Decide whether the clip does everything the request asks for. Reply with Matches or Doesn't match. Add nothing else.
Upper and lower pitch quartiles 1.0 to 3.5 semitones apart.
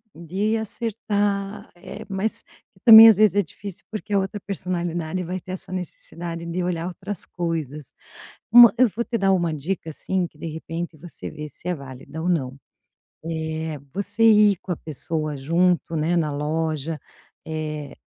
Doesn't match